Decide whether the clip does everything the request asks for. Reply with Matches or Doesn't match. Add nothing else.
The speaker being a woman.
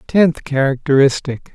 Doesn't match